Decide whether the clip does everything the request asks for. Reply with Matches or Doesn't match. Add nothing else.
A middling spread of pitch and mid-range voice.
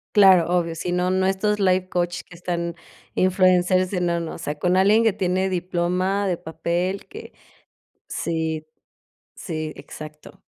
Doesn't match